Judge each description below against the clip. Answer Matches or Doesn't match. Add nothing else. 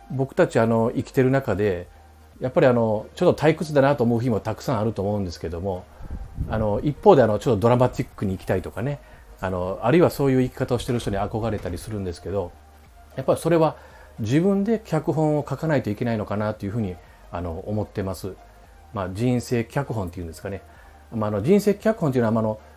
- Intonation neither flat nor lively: Doesn't match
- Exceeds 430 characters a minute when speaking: Matches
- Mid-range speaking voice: Doesn't match